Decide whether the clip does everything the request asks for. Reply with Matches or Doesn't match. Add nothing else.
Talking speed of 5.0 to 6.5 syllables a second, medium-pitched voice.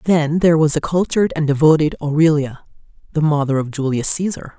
Matches